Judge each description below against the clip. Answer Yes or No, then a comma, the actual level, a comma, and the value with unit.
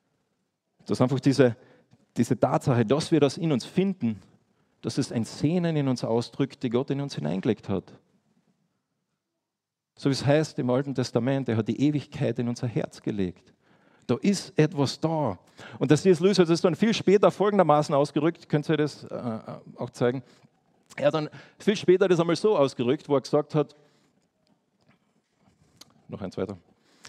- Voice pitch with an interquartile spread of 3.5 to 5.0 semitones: Yes, average, 4.2 semitones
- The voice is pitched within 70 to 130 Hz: No, medium, 140 Hz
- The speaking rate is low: No, average, 175 wpm